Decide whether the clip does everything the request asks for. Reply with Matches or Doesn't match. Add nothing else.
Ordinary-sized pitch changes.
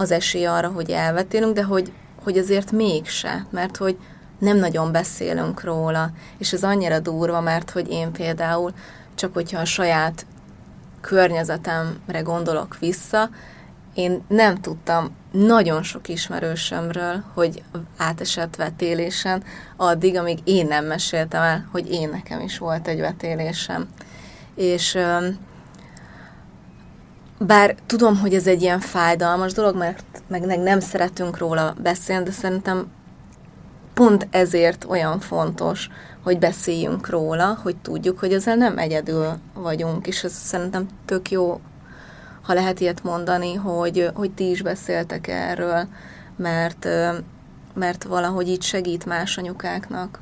Doesn't match